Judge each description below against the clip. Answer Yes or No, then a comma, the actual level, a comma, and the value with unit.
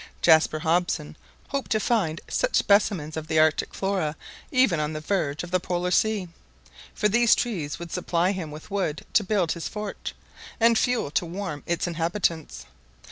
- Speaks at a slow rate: No, average, 170 wpm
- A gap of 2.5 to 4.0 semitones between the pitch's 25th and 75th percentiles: No, average, 4.4 semitones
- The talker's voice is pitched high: No, medium, 175 Hz